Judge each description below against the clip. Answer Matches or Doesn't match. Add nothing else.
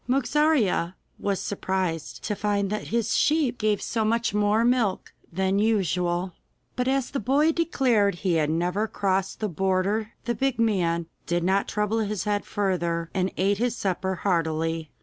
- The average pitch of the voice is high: Matches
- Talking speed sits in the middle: Matches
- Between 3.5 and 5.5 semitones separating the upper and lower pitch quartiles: Matches